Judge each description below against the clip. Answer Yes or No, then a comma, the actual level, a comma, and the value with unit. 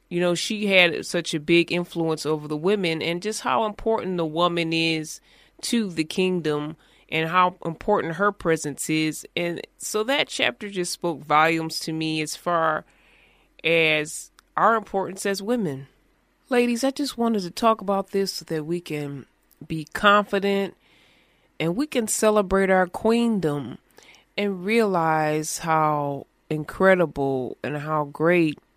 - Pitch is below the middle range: No, medium, 175 Hz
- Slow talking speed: No, average, 145 wpm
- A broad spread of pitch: No, average, 4.4 semitones